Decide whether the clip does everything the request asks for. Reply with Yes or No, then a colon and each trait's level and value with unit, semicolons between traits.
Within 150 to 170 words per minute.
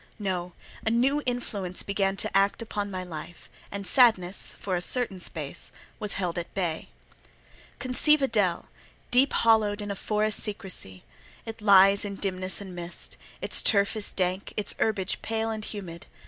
Yes: average, 160 wpm